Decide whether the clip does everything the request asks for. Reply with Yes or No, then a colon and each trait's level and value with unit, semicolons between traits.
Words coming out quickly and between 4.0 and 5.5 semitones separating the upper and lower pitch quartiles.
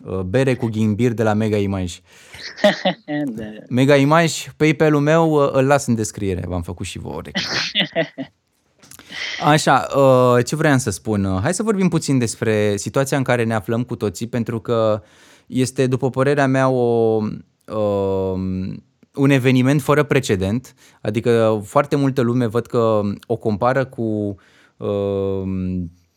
No: average, 140 wpm; average, 4.5 semitones